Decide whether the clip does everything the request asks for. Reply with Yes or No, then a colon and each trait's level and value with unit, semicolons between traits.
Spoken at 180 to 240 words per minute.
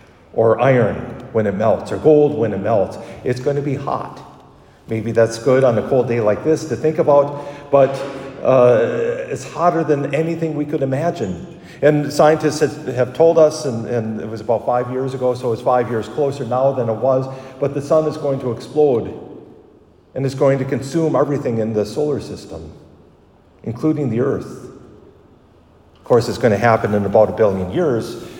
Yes: average, 190 wpm